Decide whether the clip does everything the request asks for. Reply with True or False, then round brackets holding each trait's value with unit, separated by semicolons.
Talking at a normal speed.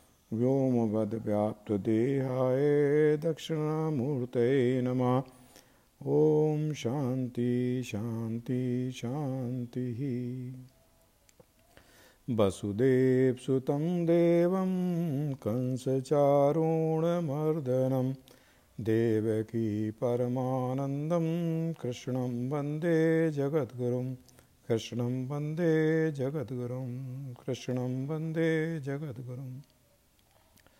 False (40 wpm)